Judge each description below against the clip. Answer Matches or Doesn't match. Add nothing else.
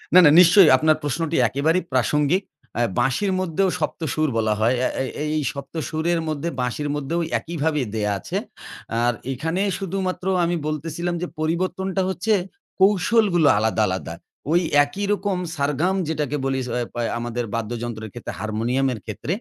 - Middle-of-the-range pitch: Matches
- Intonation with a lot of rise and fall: Matches